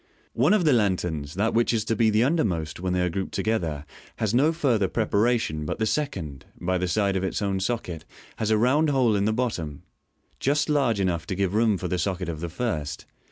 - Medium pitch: No, low, 100 Hz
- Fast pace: Yes, fast, 230 wpm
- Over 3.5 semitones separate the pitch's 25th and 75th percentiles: Yes, average, 4.9 semitones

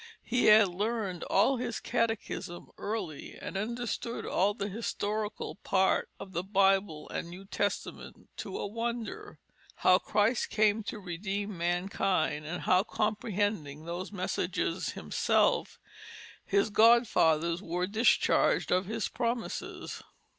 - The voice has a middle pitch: No, high, 200 Hz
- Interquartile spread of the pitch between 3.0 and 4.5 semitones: Yes, average, 3.5 semitones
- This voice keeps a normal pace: No, slow, 120 wpm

